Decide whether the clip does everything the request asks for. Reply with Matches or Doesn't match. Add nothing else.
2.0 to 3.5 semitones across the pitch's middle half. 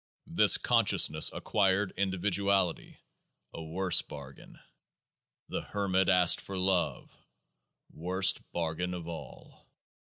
Matches